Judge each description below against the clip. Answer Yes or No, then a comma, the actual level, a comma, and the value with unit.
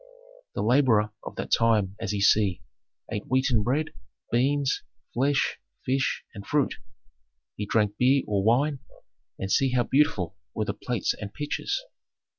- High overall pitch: No, low, 120 Hz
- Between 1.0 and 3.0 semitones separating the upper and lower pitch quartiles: No, average, 4.5 semitones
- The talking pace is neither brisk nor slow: Yes, average, 145 wpm